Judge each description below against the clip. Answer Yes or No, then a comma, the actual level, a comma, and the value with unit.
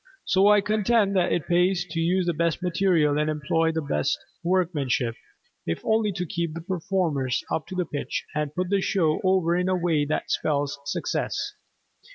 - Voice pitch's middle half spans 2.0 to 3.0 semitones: No, average, 3.6 semitones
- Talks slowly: No, average, 180 wpm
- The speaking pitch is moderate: Yes, medium, 170 Hz